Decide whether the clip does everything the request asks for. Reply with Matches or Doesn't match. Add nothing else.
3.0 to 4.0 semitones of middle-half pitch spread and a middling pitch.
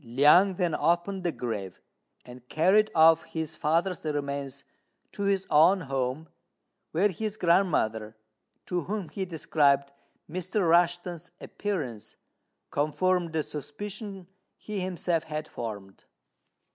Doesn't match